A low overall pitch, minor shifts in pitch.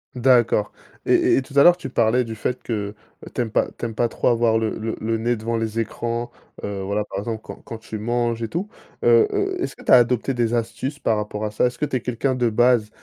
Yes: low, 115 Hz; narrow, 2.2 semitones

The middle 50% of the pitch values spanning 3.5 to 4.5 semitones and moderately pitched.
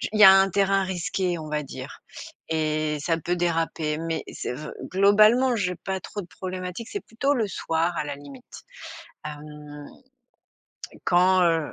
Yes: average, 4.0 semitones; medium, 175 Hz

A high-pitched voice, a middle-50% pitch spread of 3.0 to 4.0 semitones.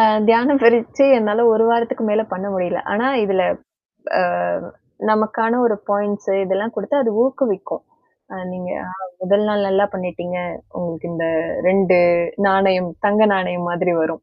Yes: high, 200 Hz; average, 3.5 semitones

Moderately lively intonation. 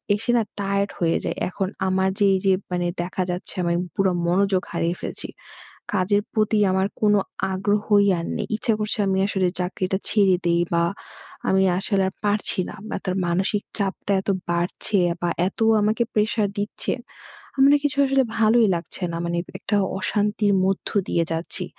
No: narrow, 2.3 semitones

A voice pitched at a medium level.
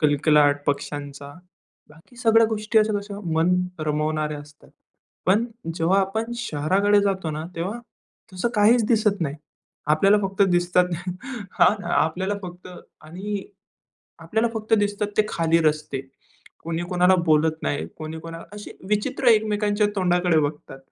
Yes: medium, 180 Hz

